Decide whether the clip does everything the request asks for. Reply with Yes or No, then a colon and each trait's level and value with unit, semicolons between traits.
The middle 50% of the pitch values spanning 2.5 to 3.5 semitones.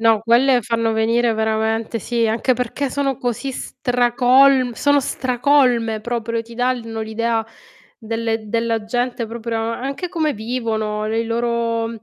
No: narrow, 1.9 semitones